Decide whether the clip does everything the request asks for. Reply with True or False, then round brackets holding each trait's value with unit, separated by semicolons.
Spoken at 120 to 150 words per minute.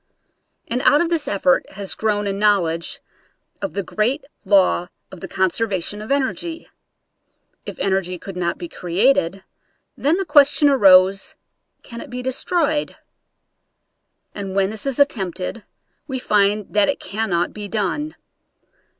True (140 wpm)